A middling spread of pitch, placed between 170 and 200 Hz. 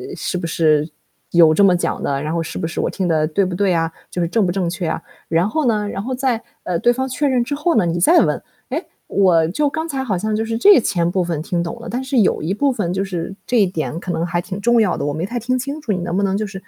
No: wide, 5.8 semitones; high, 190 Hz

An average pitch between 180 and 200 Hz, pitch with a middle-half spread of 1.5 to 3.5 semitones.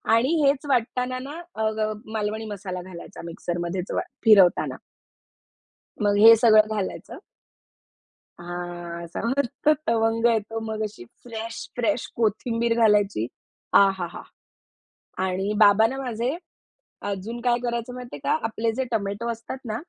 No: high, 220 Hz; average, 3.0 semitones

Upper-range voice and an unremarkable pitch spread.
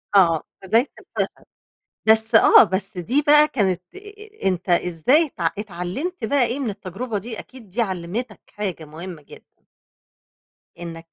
No: high, 210 Hz; wide, 6.2 semitones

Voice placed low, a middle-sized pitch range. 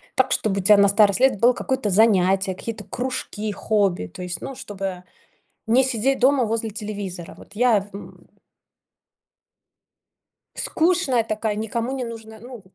No: high, 215 Hz; average, 3.7 semitones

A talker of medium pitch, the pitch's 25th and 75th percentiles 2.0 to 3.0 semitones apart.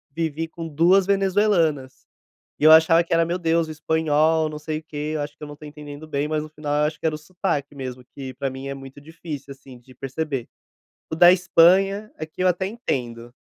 Yes: medium, 155 Hz; narrow, 2.6 semitones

